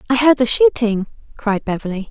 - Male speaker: No, female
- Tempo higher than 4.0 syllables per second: Yes, 5.6 syllables/s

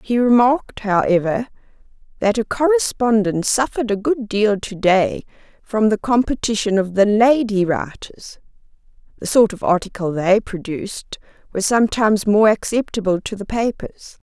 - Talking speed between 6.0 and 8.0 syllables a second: No, 4.9 syllables/s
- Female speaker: Yes, female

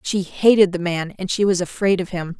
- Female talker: Yes, female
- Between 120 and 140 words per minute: No, fast, 250 wpm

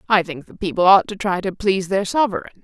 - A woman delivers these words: Yes, female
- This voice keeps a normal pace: No, fast, 250 wpm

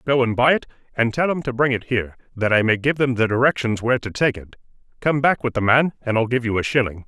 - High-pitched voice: No, low, 120 Hz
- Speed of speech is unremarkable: No, fast, 280 wpm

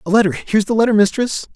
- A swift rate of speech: Yes, fast, 230 wpm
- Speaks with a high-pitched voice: Yes, high, 210 Hz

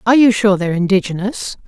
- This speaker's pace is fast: No, average, 180 wpm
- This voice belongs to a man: No, female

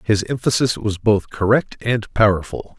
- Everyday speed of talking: Yes, average, 150 wpm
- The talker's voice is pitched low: Yes, low, 105 Hz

